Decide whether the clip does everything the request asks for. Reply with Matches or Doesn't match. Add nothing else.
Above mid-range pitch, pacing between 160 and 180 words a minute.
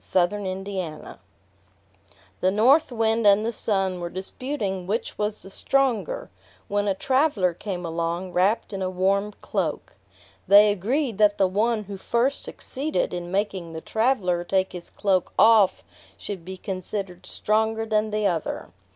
Doesn't match